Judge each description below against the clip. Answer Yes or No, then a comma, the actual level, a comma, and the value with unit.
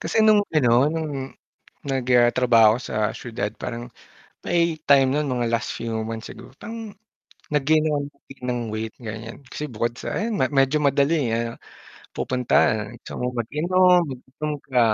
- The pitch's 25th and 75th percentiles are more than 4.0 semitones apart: Yes, average, 4.4 semitones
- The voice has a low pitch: Yes, low, 130 Hz